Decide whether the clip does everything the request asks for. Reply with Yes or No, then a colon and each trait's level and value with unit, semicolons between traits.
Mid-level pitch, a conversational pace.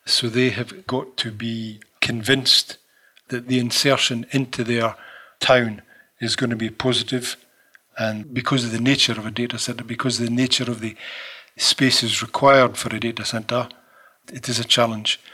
No: low, 120 Hz; average, 170 wpm